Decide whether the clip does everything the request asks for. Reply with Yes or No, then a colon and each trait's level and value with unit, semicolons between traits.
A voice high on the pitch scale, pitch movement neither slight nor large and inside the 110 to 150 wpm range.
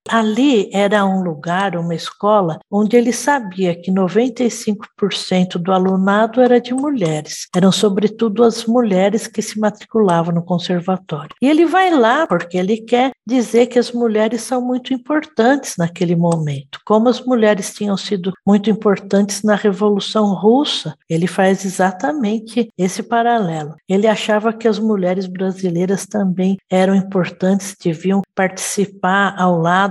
Yes: high, 205 Hz; average, 3.5 semitones; average, 140 wpm